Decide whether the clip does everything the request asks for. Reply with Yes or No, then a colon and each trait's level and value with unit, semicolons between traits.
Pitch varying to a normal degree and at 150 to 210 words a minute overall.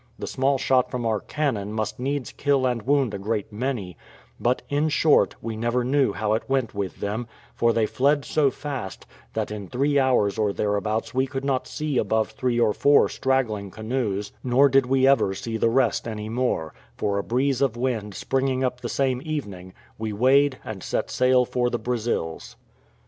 Yes: average, 3.8 semitones; average, 190 wpm